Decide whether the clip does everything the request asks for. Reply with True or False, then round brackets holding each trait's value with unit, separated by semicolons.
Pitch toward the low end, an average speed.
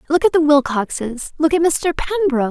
False (300 Hz; 190 wpm)